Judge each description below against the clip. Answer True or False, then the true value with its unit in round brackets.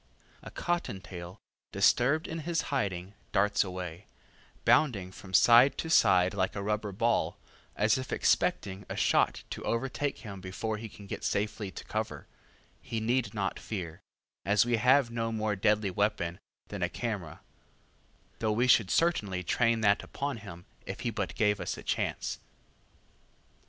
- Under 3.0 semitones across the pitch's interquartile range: False (3.7 semitones)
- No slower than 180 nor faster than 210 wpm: False (155 wpm)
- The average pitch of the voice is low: True (105 Hz)